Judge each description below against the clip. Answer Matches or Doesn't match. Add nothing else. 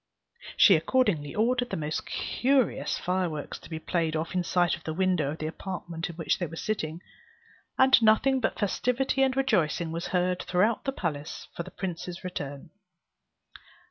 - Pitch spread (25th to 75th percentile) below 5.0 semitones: Doesn't match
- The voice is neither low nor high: Matches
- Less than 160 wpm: Doesn't match